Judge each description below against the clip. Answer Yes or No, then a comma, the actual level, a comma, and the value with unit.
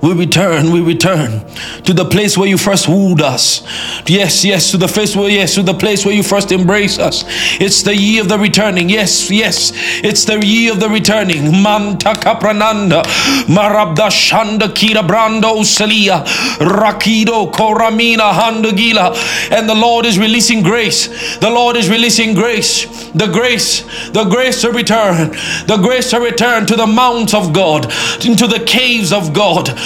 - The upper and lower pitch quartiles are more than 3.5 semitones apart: No, average, 3.2 semitones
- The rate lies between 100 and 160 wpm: Yes, average, 155 wpm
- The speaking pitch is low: No, high, 210 Hz